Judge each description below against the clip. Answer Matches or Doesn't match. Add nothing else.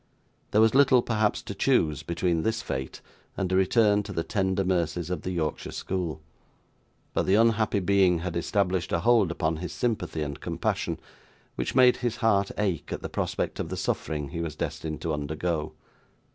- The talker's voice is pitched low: Matches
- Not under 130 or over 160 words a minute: Doesn't match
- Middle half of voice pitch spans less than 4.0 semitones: Doesn't match